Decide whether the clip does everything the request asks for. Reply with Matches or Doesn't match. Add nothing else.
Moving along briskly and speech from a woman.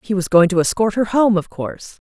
Matches